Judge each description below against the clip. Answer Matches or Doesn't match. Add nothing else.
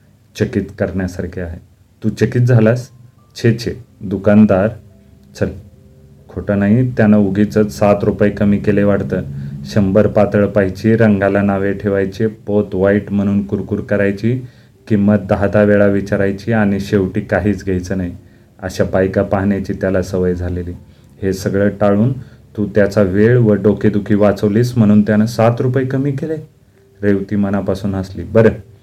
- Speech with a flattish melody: Matches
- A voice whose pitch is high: Doesn't match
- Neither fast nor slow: Doesn't match